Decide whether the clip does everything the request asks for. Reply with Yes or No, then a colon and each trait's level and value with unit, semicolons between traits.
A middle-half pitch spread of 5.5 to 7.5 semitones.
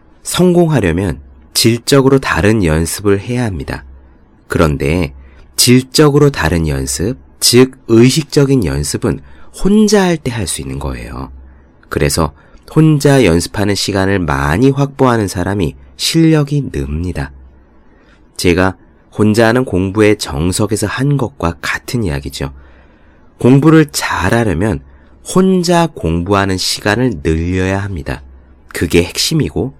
No: wide, 9.0 semitones